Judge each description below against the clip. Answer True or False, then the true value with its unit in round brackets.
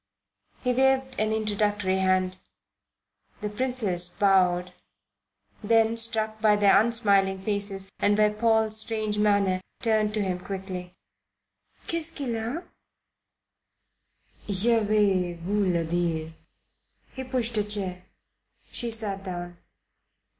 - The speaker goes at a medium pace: False (120 wpm)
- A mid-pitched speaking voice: False (210 Hz)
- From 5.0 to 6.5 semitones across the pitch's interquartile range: False (3.0 semitones)